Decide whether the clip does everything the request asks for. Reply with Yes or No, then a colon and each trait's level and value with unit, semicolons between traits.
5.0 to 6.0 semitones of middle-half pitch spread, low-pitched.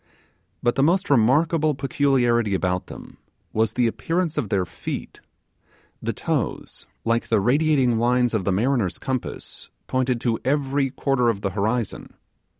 No: average, 3.7 semitones; low, 125 Hz